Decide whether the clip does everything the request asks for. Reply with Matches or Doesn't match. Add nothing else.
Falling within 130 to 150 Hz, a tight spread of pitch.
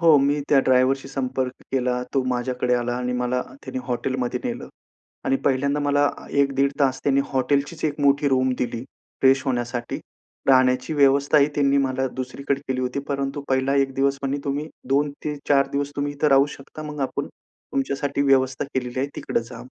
Matches